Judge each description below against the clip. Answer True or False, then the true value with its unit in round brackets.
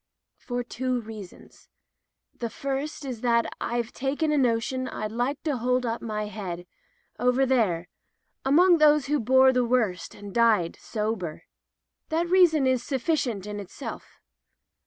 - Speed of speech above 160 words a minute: False (140 wpm)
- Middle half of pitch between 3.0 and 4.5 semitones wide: True (3.8 semitones)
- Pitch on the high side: True (245 Hz)